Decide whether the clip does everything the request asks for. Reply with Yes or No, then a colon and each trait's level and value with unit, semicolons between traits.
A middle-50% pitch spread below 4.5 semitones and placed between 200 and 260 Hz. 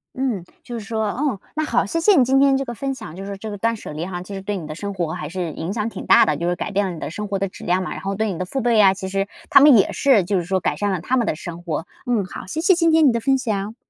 No: average, 5.1 semitones; high, 205 Hz